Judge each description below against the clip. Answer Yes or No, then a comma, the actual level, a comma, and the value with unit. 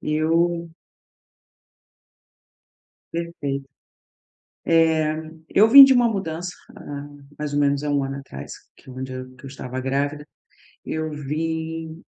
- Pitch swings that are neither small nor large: Yes, average, 3.1 semitones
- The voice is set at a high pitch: No, medium, 150 Hz